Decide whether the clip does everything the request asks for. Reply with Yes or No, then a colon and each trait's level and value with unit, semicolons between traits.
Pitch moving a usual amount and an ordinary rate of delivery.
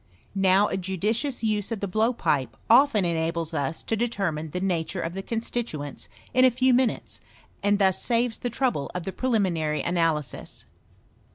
No: wide, 5.9 semitones; average, 165 wpm